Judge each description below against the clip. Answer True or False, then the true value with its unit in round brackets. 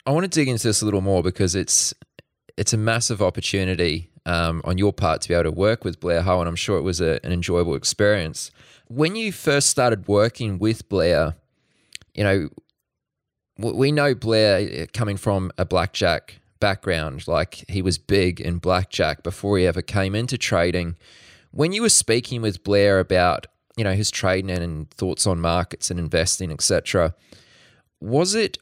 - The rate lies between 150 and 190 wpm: True (180 wpm)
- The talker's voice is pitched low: True (95 Hz)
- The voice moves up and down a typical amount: True (4.2 semitones)